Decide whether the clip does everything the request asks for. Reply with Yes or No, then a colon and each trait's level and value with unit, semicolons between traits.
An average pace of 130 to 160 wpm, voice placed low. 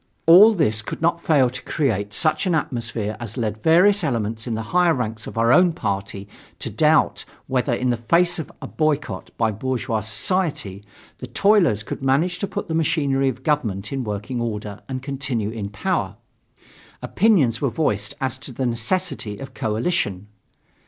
No: average, 170 wpm; low, 125 Hz